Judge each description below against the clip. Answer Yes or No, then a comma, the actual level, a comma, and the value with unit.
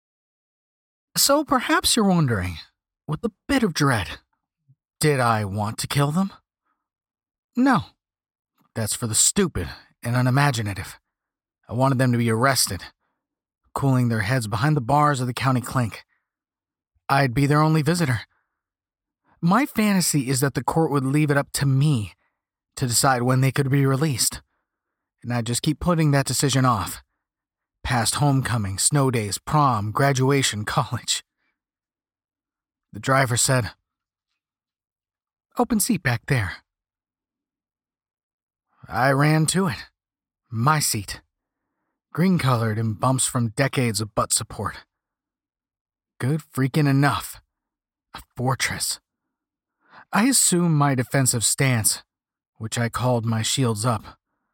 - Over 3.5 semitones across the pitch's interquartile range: Yes, average, 4.4 semitones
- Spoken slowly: Yes, slow, 125 wpm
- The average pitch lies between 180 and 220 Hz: No, low, 135 Hz